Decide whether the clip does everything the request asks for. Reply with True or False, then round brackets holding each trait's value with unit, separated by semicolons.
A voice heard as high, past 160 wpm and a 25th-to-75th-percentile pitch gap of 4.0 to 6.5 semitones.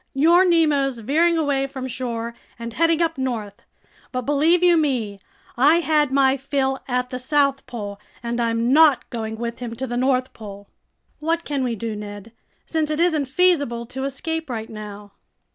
True (265 Hz; 175 wpm; 4.6 semitones)